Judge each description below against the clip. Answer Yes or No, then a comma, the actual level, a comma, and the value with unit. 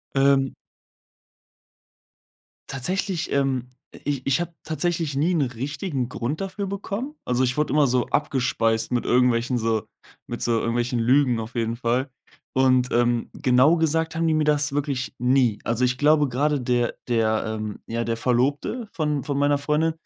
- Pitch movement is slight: No, average, 3.8 semitones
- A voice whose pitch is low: Yes, low, 130 Hz